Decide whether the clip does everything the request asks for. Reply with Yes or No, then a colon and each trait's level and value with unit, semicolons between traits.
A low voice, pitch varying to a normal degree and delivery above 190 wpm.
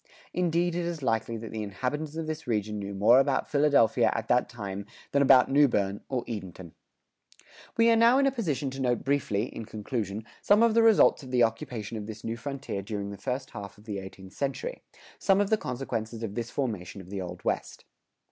No: low, 120 Hz; wide, 5.9 semitones; fast, 205 wpm